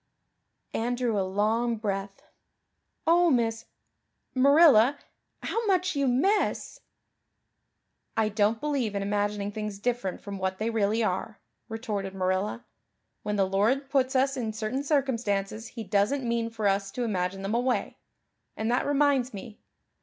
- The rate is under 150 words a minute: Yes, average, 140 wpm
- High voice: Yes, high, 225 Hz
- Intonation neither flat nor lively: Yes, average, 4.2 semitones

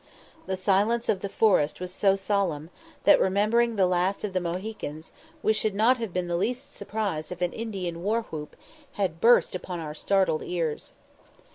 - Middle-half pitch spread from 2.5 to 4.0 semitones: Yes, average, 3.6 semitones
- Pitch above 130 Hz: Yes, high, 190 Hz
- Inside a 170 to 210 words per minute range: Yes, average, 175 wpm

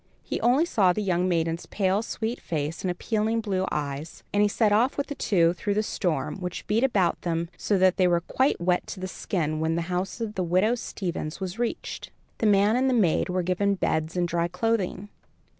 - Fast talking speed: Yes, fast, 210 wpm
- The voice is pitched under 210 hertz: Yes, medium, 185 Hz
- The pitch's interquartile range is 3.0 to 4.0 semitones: Yes, average, 3.7 semitones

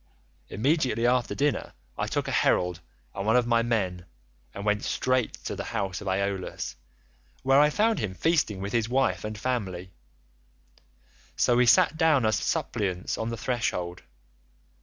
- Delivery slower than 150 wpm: No, average, 160 wpm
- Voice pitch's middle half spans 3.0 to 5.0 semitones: Yes, average, 4.7 semitones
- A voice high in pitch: No, low, 115 Hz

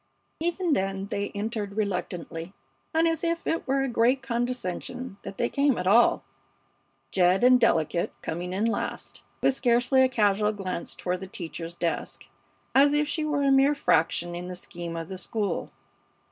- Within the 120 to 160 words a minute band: No, average, 170 wpm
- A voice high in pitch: Yes, high, 215 Hz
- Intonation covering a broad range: Yes, wide, 6.8 semitones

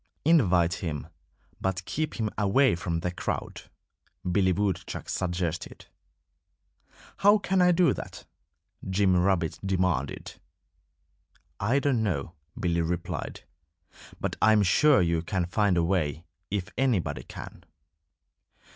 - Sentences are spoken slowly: Yes, slow, 120 wpm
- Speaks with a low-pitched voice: Yes, very low, 95 Hz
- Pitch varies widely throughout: No, average, 4.1 semitones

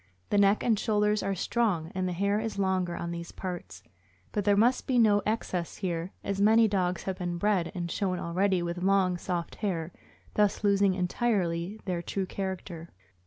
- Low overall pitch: No, high, 190 Hz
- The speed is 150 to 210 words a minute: Yes, average, 180 wpm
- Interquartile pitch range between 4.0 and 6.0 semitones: No, average, 2.8 semitones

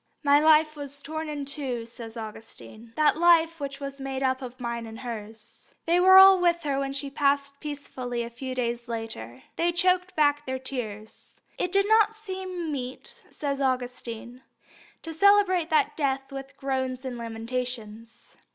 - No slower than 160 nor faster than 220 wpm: Yes, average, 170 wpm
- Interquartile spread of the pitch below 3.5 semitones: No, average, 4.7 semitones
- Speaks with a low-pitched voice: No, very high, 275 Hz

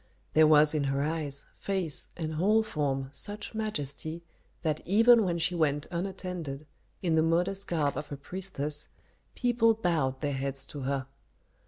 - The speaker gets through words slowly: No, average, 155 wpm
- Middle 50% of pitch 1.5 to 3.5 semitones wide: No, average, 4.8 semitones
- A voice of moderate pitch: Yes, medium, 160 Hz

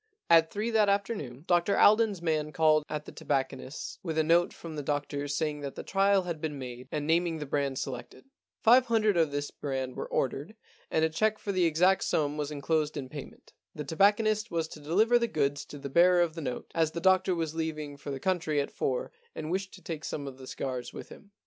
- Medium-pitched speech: Yes, medium, 160 Hz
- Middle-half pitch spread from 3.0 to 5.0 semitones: Yes, average, 4.4 semitones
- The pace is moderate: No, fast, 225 wpm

